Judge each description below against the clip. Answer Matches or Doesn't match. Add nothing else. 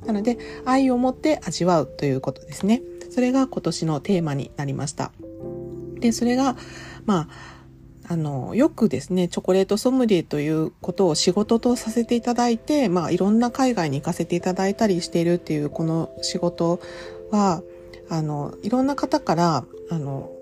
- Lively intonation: Matches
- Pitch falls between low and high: Matches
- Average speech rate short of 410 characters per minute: Matches